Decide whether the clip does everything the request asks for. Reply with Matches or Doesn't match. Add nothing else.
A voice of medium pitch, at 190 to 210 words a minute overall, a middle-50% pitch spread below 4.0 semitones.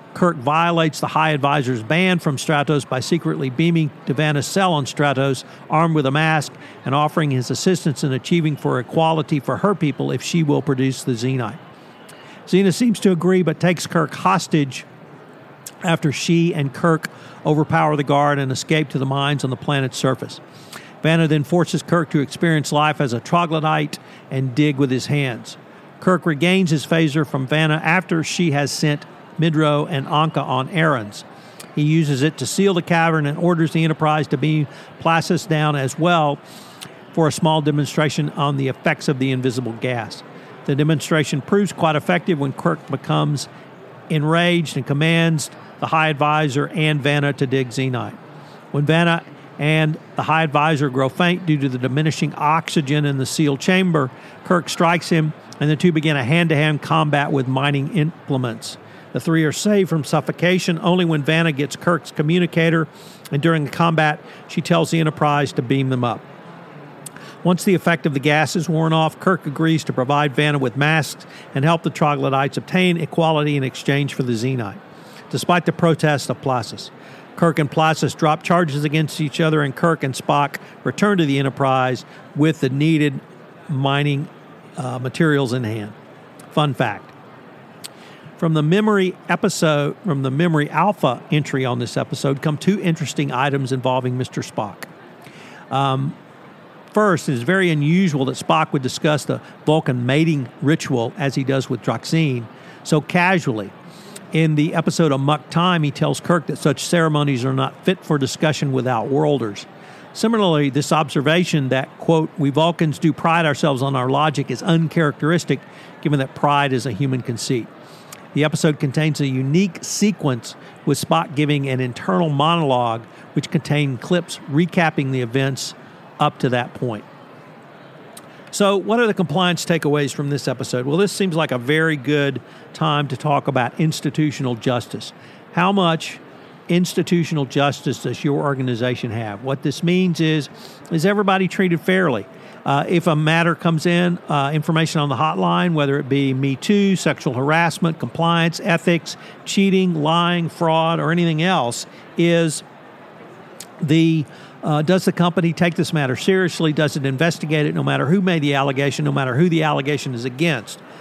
Doesn't match